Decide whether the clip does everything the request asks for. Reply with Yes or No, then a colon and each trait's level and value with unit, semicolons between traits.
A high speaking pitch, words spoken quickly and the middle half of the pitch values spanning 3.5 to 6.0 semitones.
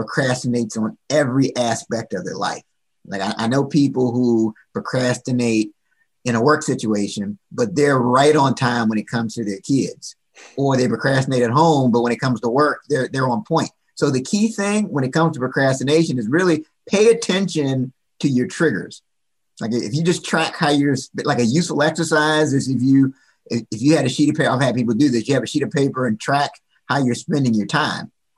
No: low, 135 Hz; fast, 210 wpm; average, 4.0 semitones